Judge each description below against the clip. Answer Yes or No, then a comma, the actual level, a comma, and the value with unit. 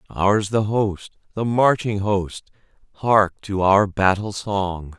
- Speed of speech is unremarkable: No, slow, 120 wpm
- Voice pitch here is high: No, low, 100 Hz